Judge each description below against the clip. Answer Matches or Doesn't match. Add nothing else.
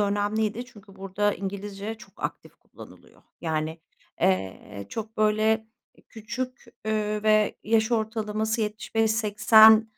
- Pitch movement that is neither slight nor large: Doesn't match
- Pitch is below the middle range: Doesn't match